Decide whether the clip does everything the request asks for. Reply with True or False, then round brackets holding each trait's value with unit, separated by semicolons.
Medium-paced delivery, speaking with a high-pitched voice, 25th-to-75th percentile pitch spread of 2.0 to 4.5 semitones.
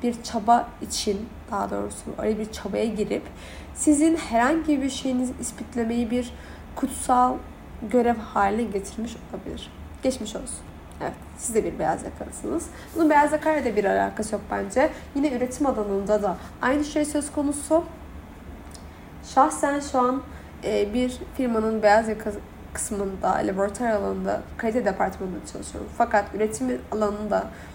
True (130 wpm; 235 Hz; 4.2 semitones)